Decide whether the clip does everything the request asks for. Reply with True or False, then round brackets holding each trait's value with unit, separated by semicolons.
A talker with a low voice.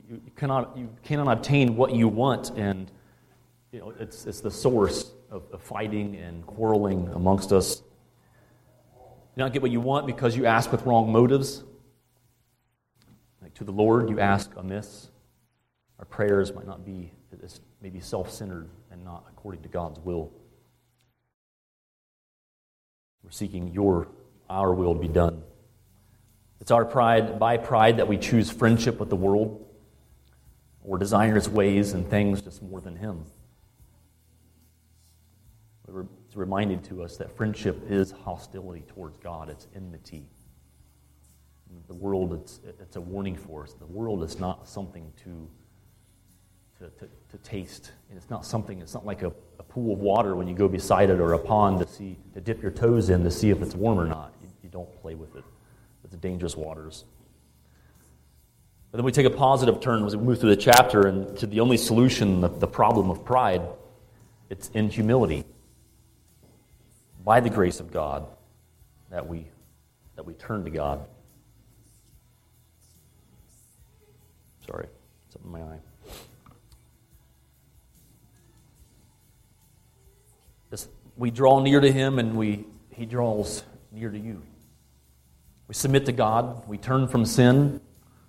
True (105 Hz)